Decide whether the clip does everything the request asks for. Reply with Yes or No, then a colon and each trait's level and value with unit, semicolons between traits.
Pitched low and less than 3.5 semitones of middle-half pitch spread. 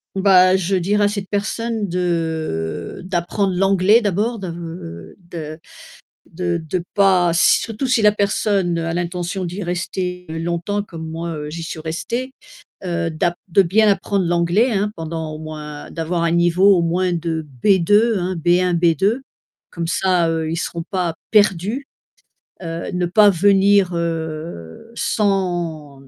No: medium, 175 Hz; average, 3.0 semitones